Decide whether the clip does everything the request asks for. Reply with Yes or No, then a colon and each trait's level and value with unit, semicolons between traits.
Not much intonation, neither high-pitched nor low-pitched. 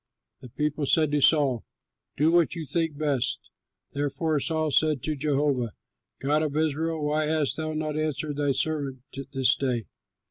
Yes: narrow, 2.0 semitones; medium, 150 Hz